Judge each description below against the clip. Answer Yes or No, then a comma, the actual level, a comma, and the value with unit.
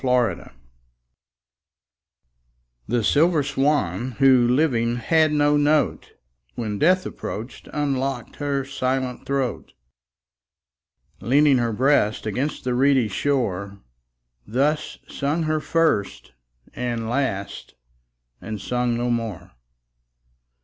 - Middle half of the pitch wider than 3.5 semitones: Yes, average, 4.0 semitones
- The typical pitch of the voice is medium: No, low, 130 Hz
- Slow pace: Yes, slow, 100 wpm